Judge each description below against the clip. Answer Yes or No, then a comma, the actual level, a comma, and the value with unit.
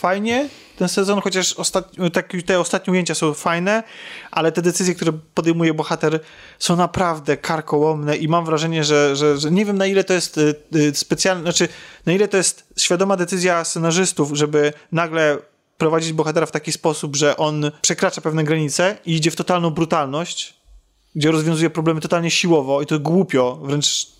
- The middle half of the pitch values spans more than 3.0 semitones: No, narrow, 2.6 semitones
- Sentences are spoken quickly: Yes, fast, 165 wpm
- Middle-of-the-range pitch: Yes, medium, 165 Hz